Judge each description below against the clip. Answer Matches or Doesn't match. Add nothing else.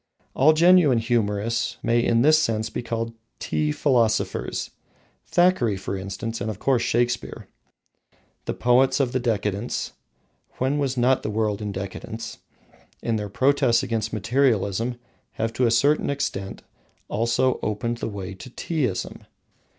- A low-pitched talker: Matches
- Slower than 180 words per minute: Matches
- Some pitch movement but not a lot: Matches